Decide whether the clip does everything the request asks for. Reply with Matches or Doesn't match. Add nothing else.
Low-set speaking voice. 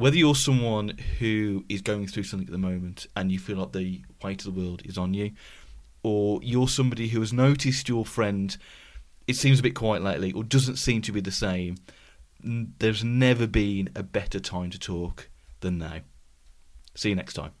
Matches